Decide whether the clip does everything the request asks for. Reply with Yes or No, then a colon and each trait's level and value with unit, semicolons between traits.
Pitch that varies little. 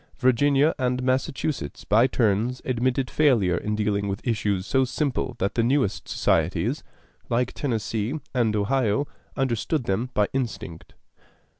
No: average, 3.9 semitones